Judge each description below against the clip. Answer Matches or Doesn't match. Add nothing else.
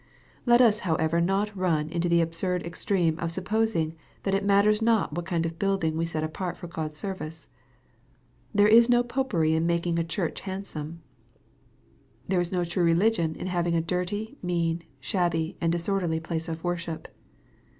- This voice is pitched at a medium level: Matches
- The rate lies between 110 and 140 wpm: Doesn't match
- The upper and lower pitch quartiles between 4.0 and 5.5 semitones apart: Doesn't match